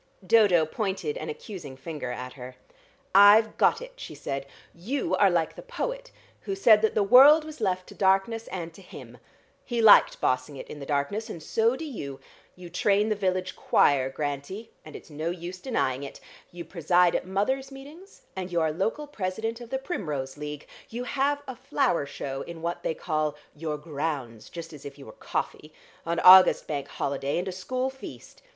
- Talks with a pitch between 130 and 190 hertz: Yes, medium, 185 Hz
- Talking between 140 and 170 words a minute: No, average, 190 wpm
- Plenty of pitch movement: Yes, wide, 7.3 semitones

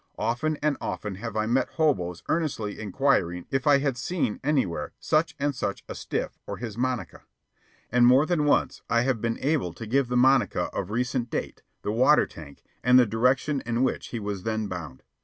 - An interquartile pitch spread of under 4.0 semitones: No, average, 4.6 semitones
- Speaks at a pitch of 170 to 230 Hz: No, low, 125 Hz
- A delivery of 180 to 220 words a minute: Yes, average, 195 wpm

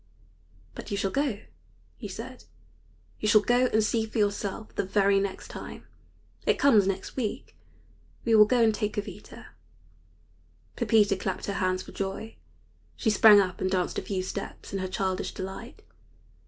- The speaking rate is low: No, average, 165 wpm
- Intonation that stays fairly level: Yes, narrow, 2.3 semitones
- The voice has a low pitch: No, high, 205 Hz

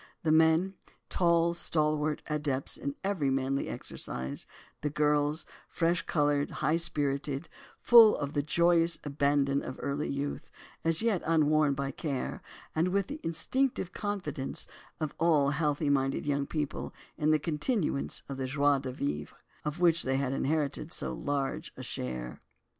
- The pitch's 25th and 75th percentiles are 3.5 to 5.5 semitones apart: No, average, 3.0 semitones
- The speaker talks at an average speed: Yes, average, 145 wpm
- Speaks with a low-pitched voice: No, medium, 150 Hz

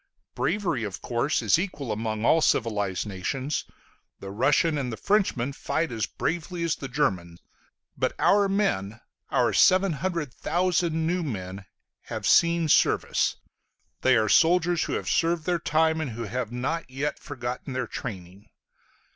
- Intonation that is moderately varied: No, wide, 7.0 semitones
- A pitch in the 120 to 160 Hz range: Yes, medium, 140 Hz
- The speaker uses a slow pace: No, average, 145 wpm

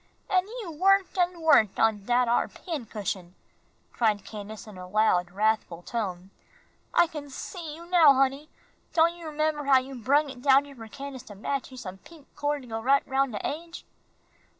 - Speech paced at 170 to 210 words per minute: Yes, average, 185 wpm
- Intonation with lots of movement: Yes, wide, 6.0 semitones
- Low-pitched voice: No, very high, 270 Hz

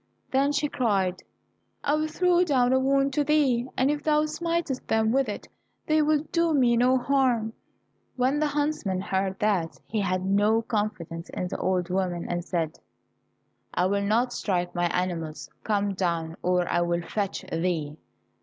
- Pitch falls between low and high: No, high, 220 Hz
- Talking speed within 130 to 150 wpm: No, average, 170 wpm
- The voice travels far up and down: Yes, wide, 7.2 semitones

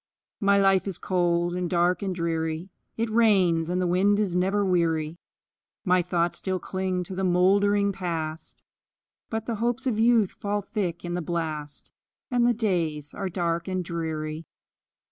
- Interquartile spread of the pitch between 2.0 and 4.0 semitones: Yes, average, 3.0 semitones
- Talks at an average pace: Yes, average, 165 wpm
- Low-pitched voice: No, medium, 180 Hz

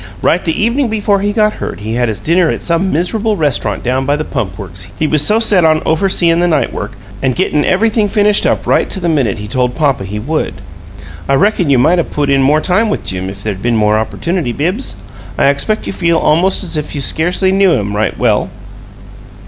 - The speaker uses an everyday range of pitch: No, wide, 7.7 semitones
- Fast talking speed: Yes, fast, 230 wpm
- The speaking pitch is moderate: Yes, medium, 155 Hz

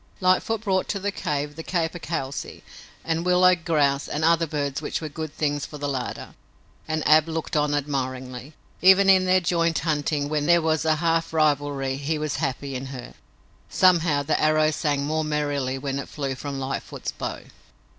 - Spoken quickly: No, average, 175 wpm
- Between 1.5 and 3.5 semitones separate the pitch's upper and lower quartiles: Yes, average, 2.8 semitones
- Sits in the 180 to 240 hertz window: No, medium, 155 Hz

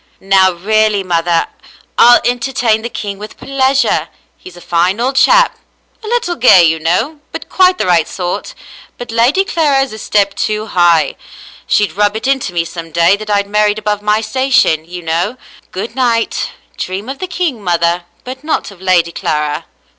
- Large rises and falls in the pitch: Yes, wide, 6.4 semitones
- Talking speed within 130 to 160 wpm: No, average, 175 wpm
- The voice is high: Yes, high, 210 Hz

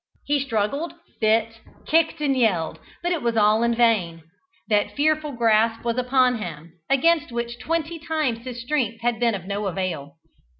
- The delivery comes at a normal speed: Yes, average, 165 wpm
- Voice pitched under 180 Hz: No, high, 235 Hz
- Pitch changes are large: No, average, 4.8 semitones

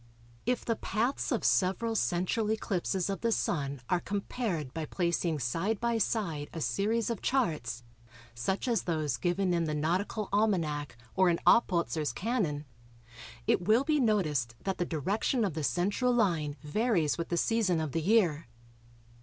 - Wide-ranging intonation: Yes, wide, 6.0 semitones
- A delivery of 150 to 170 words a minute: Yes, average, 160 wpm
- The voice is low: No, medium, 180 Hz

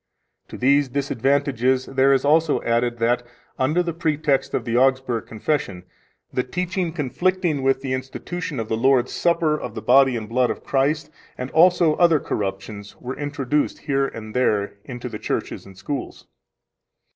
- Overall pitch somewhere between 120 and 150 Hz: Yes, low, 135 Hz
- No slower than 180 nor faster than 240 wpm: No, average, 160 wpm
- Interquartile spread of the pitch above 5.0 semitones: No, average, 3.7 semitones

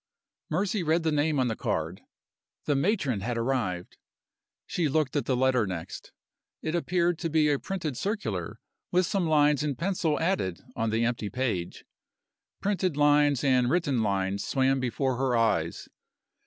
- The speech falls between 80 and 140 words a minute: No, average, 155 wpm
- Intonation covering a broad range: Yes, wide, 5.8 semitones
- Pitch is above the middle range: No, low, 135 Hz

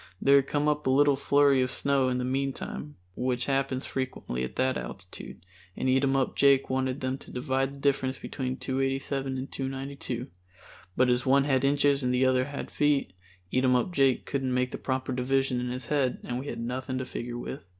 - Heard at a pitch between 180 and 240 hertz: No, low, 130 Hz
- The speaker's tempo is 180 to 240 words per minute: Yes, average, 190 wpm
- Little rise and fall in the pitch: Yes, narrow, 1.4 semitones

